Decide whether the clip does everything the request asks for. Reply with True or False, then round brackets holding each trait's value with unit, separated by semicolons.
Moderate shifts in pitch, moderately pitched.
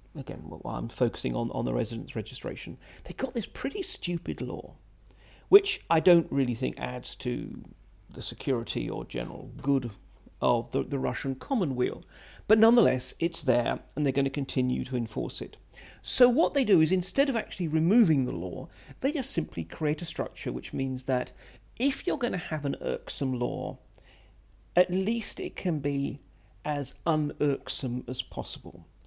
False (6.9 semitones; 145 Hz)